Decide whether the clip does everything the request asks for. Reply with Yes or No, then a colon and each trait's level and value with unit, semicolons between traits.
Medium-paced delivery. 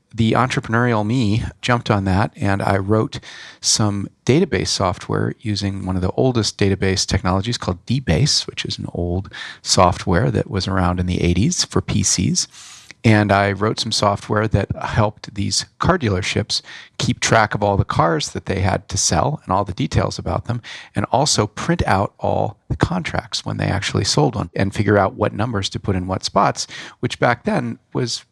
Yes: average, 185 wpm